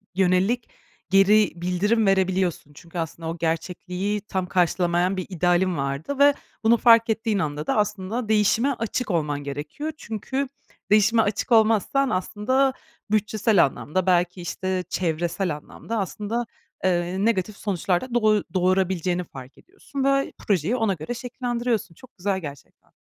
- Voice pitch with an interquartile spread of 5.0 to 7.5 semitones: No, average, 4.1 semitones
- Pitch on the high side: Yes, high, 195 Hz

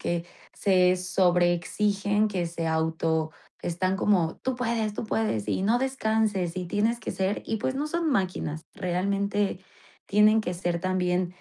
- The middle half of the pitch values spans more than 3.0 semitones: Yes, average, 3.5 semitones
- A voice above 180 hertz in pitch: Yes, high, 190 Hz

